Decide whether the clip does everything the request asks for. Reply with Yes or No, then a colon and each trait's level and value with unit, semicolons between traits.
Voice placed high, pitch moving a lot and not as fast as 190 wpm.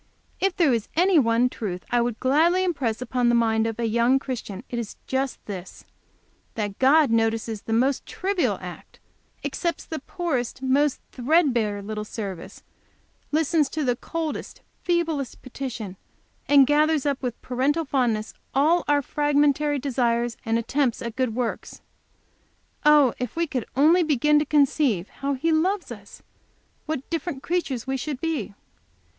No: very high, 265 Hz; average, 4.5 semitones; average, 150 wpm